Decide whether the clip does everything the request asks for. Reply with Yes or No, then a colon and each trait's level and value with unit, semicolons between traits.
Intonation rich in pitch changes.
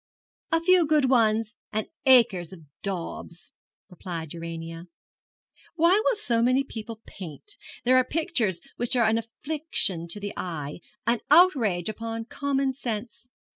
Yes: wide, 6.7 semitones